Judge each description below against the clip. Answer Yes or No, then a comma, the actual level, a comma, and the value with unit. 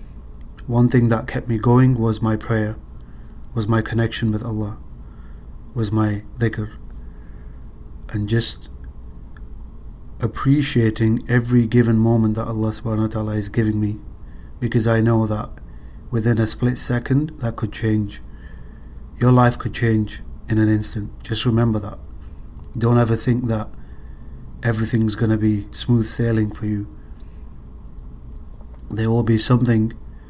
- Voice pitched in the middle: No, low, 110 Hz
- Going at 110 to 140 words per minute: Yes, slow, 135 wpm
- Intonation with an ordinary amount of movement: No, wide, 9.0 semitones